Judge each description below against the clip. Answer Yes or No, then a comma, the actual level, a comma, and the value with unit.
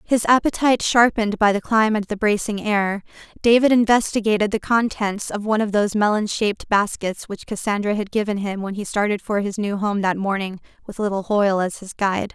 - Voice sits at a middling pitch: No, high, 210 Hz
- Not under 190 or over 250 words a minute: Yes, average, 200 wpm